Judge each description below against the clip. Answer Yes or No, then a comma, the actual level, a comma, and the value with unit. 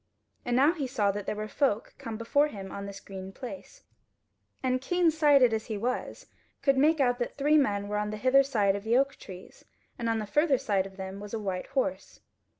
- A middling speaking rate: No, fast, 225 wpm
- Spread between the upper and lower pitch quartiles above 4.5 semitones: Yes, average, 5.2 semitones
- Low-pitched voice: No, high, 235 Hz